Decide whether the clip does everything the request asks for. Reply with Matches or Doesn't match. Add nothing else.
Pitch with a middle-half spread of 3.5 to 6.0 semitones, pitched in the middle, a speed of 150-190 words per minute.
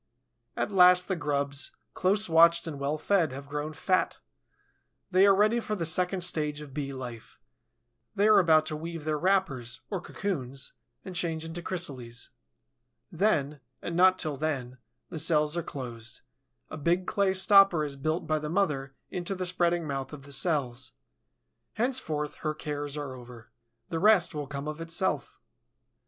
Matches